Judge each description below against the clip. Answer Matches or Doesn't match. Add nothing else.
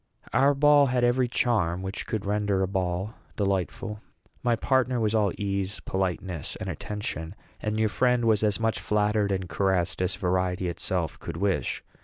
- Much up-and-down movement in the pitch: Doesn't match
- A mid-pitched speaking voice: Doesn't match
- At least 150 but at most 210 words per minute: Matches